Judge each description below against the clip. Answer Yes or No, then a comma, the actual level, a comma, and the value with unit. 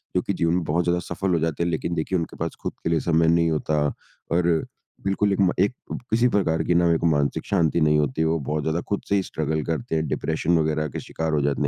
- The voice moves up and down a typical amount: No, narrow, 2.1 semitones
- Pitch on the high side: No, very low, 80 Hz